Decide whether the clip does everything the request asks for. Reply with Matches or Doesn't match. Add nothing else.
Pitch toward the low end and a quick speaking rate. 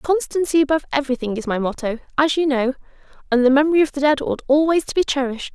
Doesn't match